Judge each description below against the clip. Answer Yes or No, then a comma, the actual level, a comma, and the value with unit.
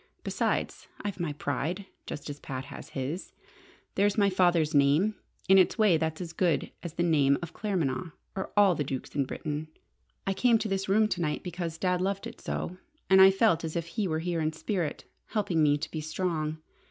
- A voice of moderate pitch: Yes, medium, 170 Hz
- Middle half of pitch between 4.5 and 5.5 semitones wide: No, average, 3.8 semitones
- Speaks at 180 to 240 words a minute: Yes, average, 200 wpm